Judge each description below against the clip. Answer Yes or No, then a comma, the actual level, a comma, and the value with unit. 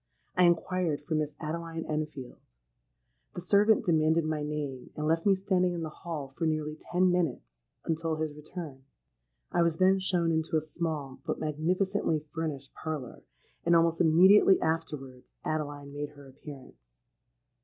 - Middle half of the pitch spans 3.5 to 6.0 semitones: No, narrow, 2.6 semitones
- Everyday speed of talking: Yes, average, 150 wpm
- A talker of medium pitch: Yes, medium, 160 Hz